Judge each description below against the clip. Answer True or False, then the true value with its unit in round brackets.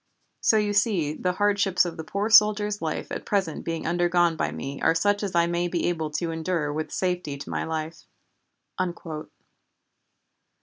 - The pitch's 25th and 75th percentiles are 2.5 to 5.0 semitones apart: True (4.0 semitones)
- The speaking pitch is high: False (175 Hz)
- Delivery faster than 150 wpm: True (170 wpm)